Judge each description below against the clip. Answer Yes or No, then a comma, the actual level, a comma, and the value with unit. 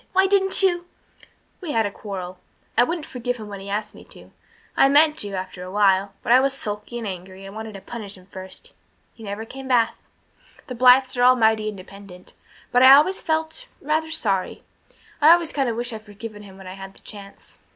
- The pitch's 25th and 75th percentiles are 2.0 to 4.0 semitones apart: No, wide, 5.5 semitones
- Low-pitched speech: No, high, 220 Hz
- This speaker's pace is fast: Yes, fast, 215 wpm